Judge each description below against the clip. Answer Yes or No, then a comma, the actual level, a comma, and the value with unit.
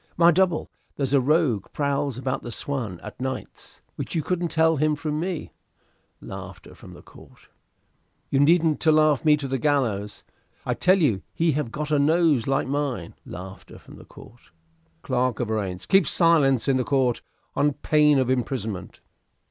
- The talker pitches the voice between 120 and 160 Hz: Yes, medium, 140 Hz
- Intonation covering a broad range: No, average, 3.7 semitones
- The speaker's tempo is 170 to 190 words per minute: No, average, 155 wpm